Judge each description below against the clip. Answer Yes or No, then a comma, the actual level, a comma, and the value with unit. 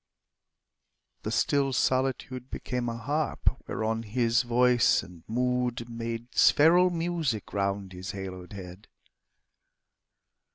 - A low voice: Yes, low, 120 Hz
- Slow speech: Yes, slow, 100 wpm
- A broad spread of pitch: No, average, 4.0 semitones